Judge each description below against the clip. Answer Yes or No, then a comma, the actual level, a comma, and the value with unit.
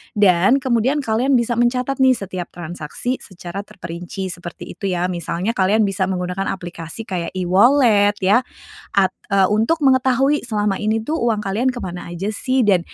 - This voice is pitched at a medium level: No, high, 205 Hz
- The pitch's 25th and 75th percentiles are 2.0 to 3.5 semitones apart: No, average, 5.0 semitones